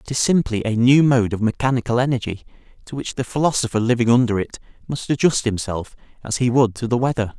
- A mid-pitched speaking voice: No, low, 120 Hz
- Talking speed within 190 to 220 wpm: Yes, fast, 205 wpm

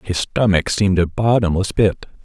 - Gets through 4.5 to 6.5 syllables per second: Yes, 5.0 syllables/s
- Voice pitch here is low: Yes, low, 100 Hz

